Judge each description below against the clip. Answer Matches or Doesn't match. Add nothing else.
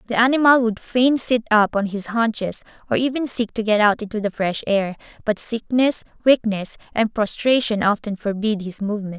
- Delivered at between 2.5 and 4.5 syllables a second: Doesn't match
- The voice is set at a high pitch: Matches